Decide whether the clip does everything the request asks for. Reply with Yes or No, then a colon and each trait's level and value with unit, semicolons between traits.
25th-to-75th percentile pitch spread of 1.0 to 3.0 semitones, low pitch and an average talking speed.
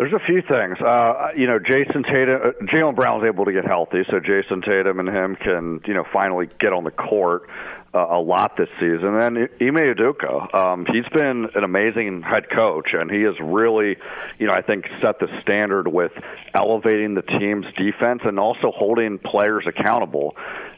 No: average, 4.2 semitones; low, 110 Hz; average, 190 wpm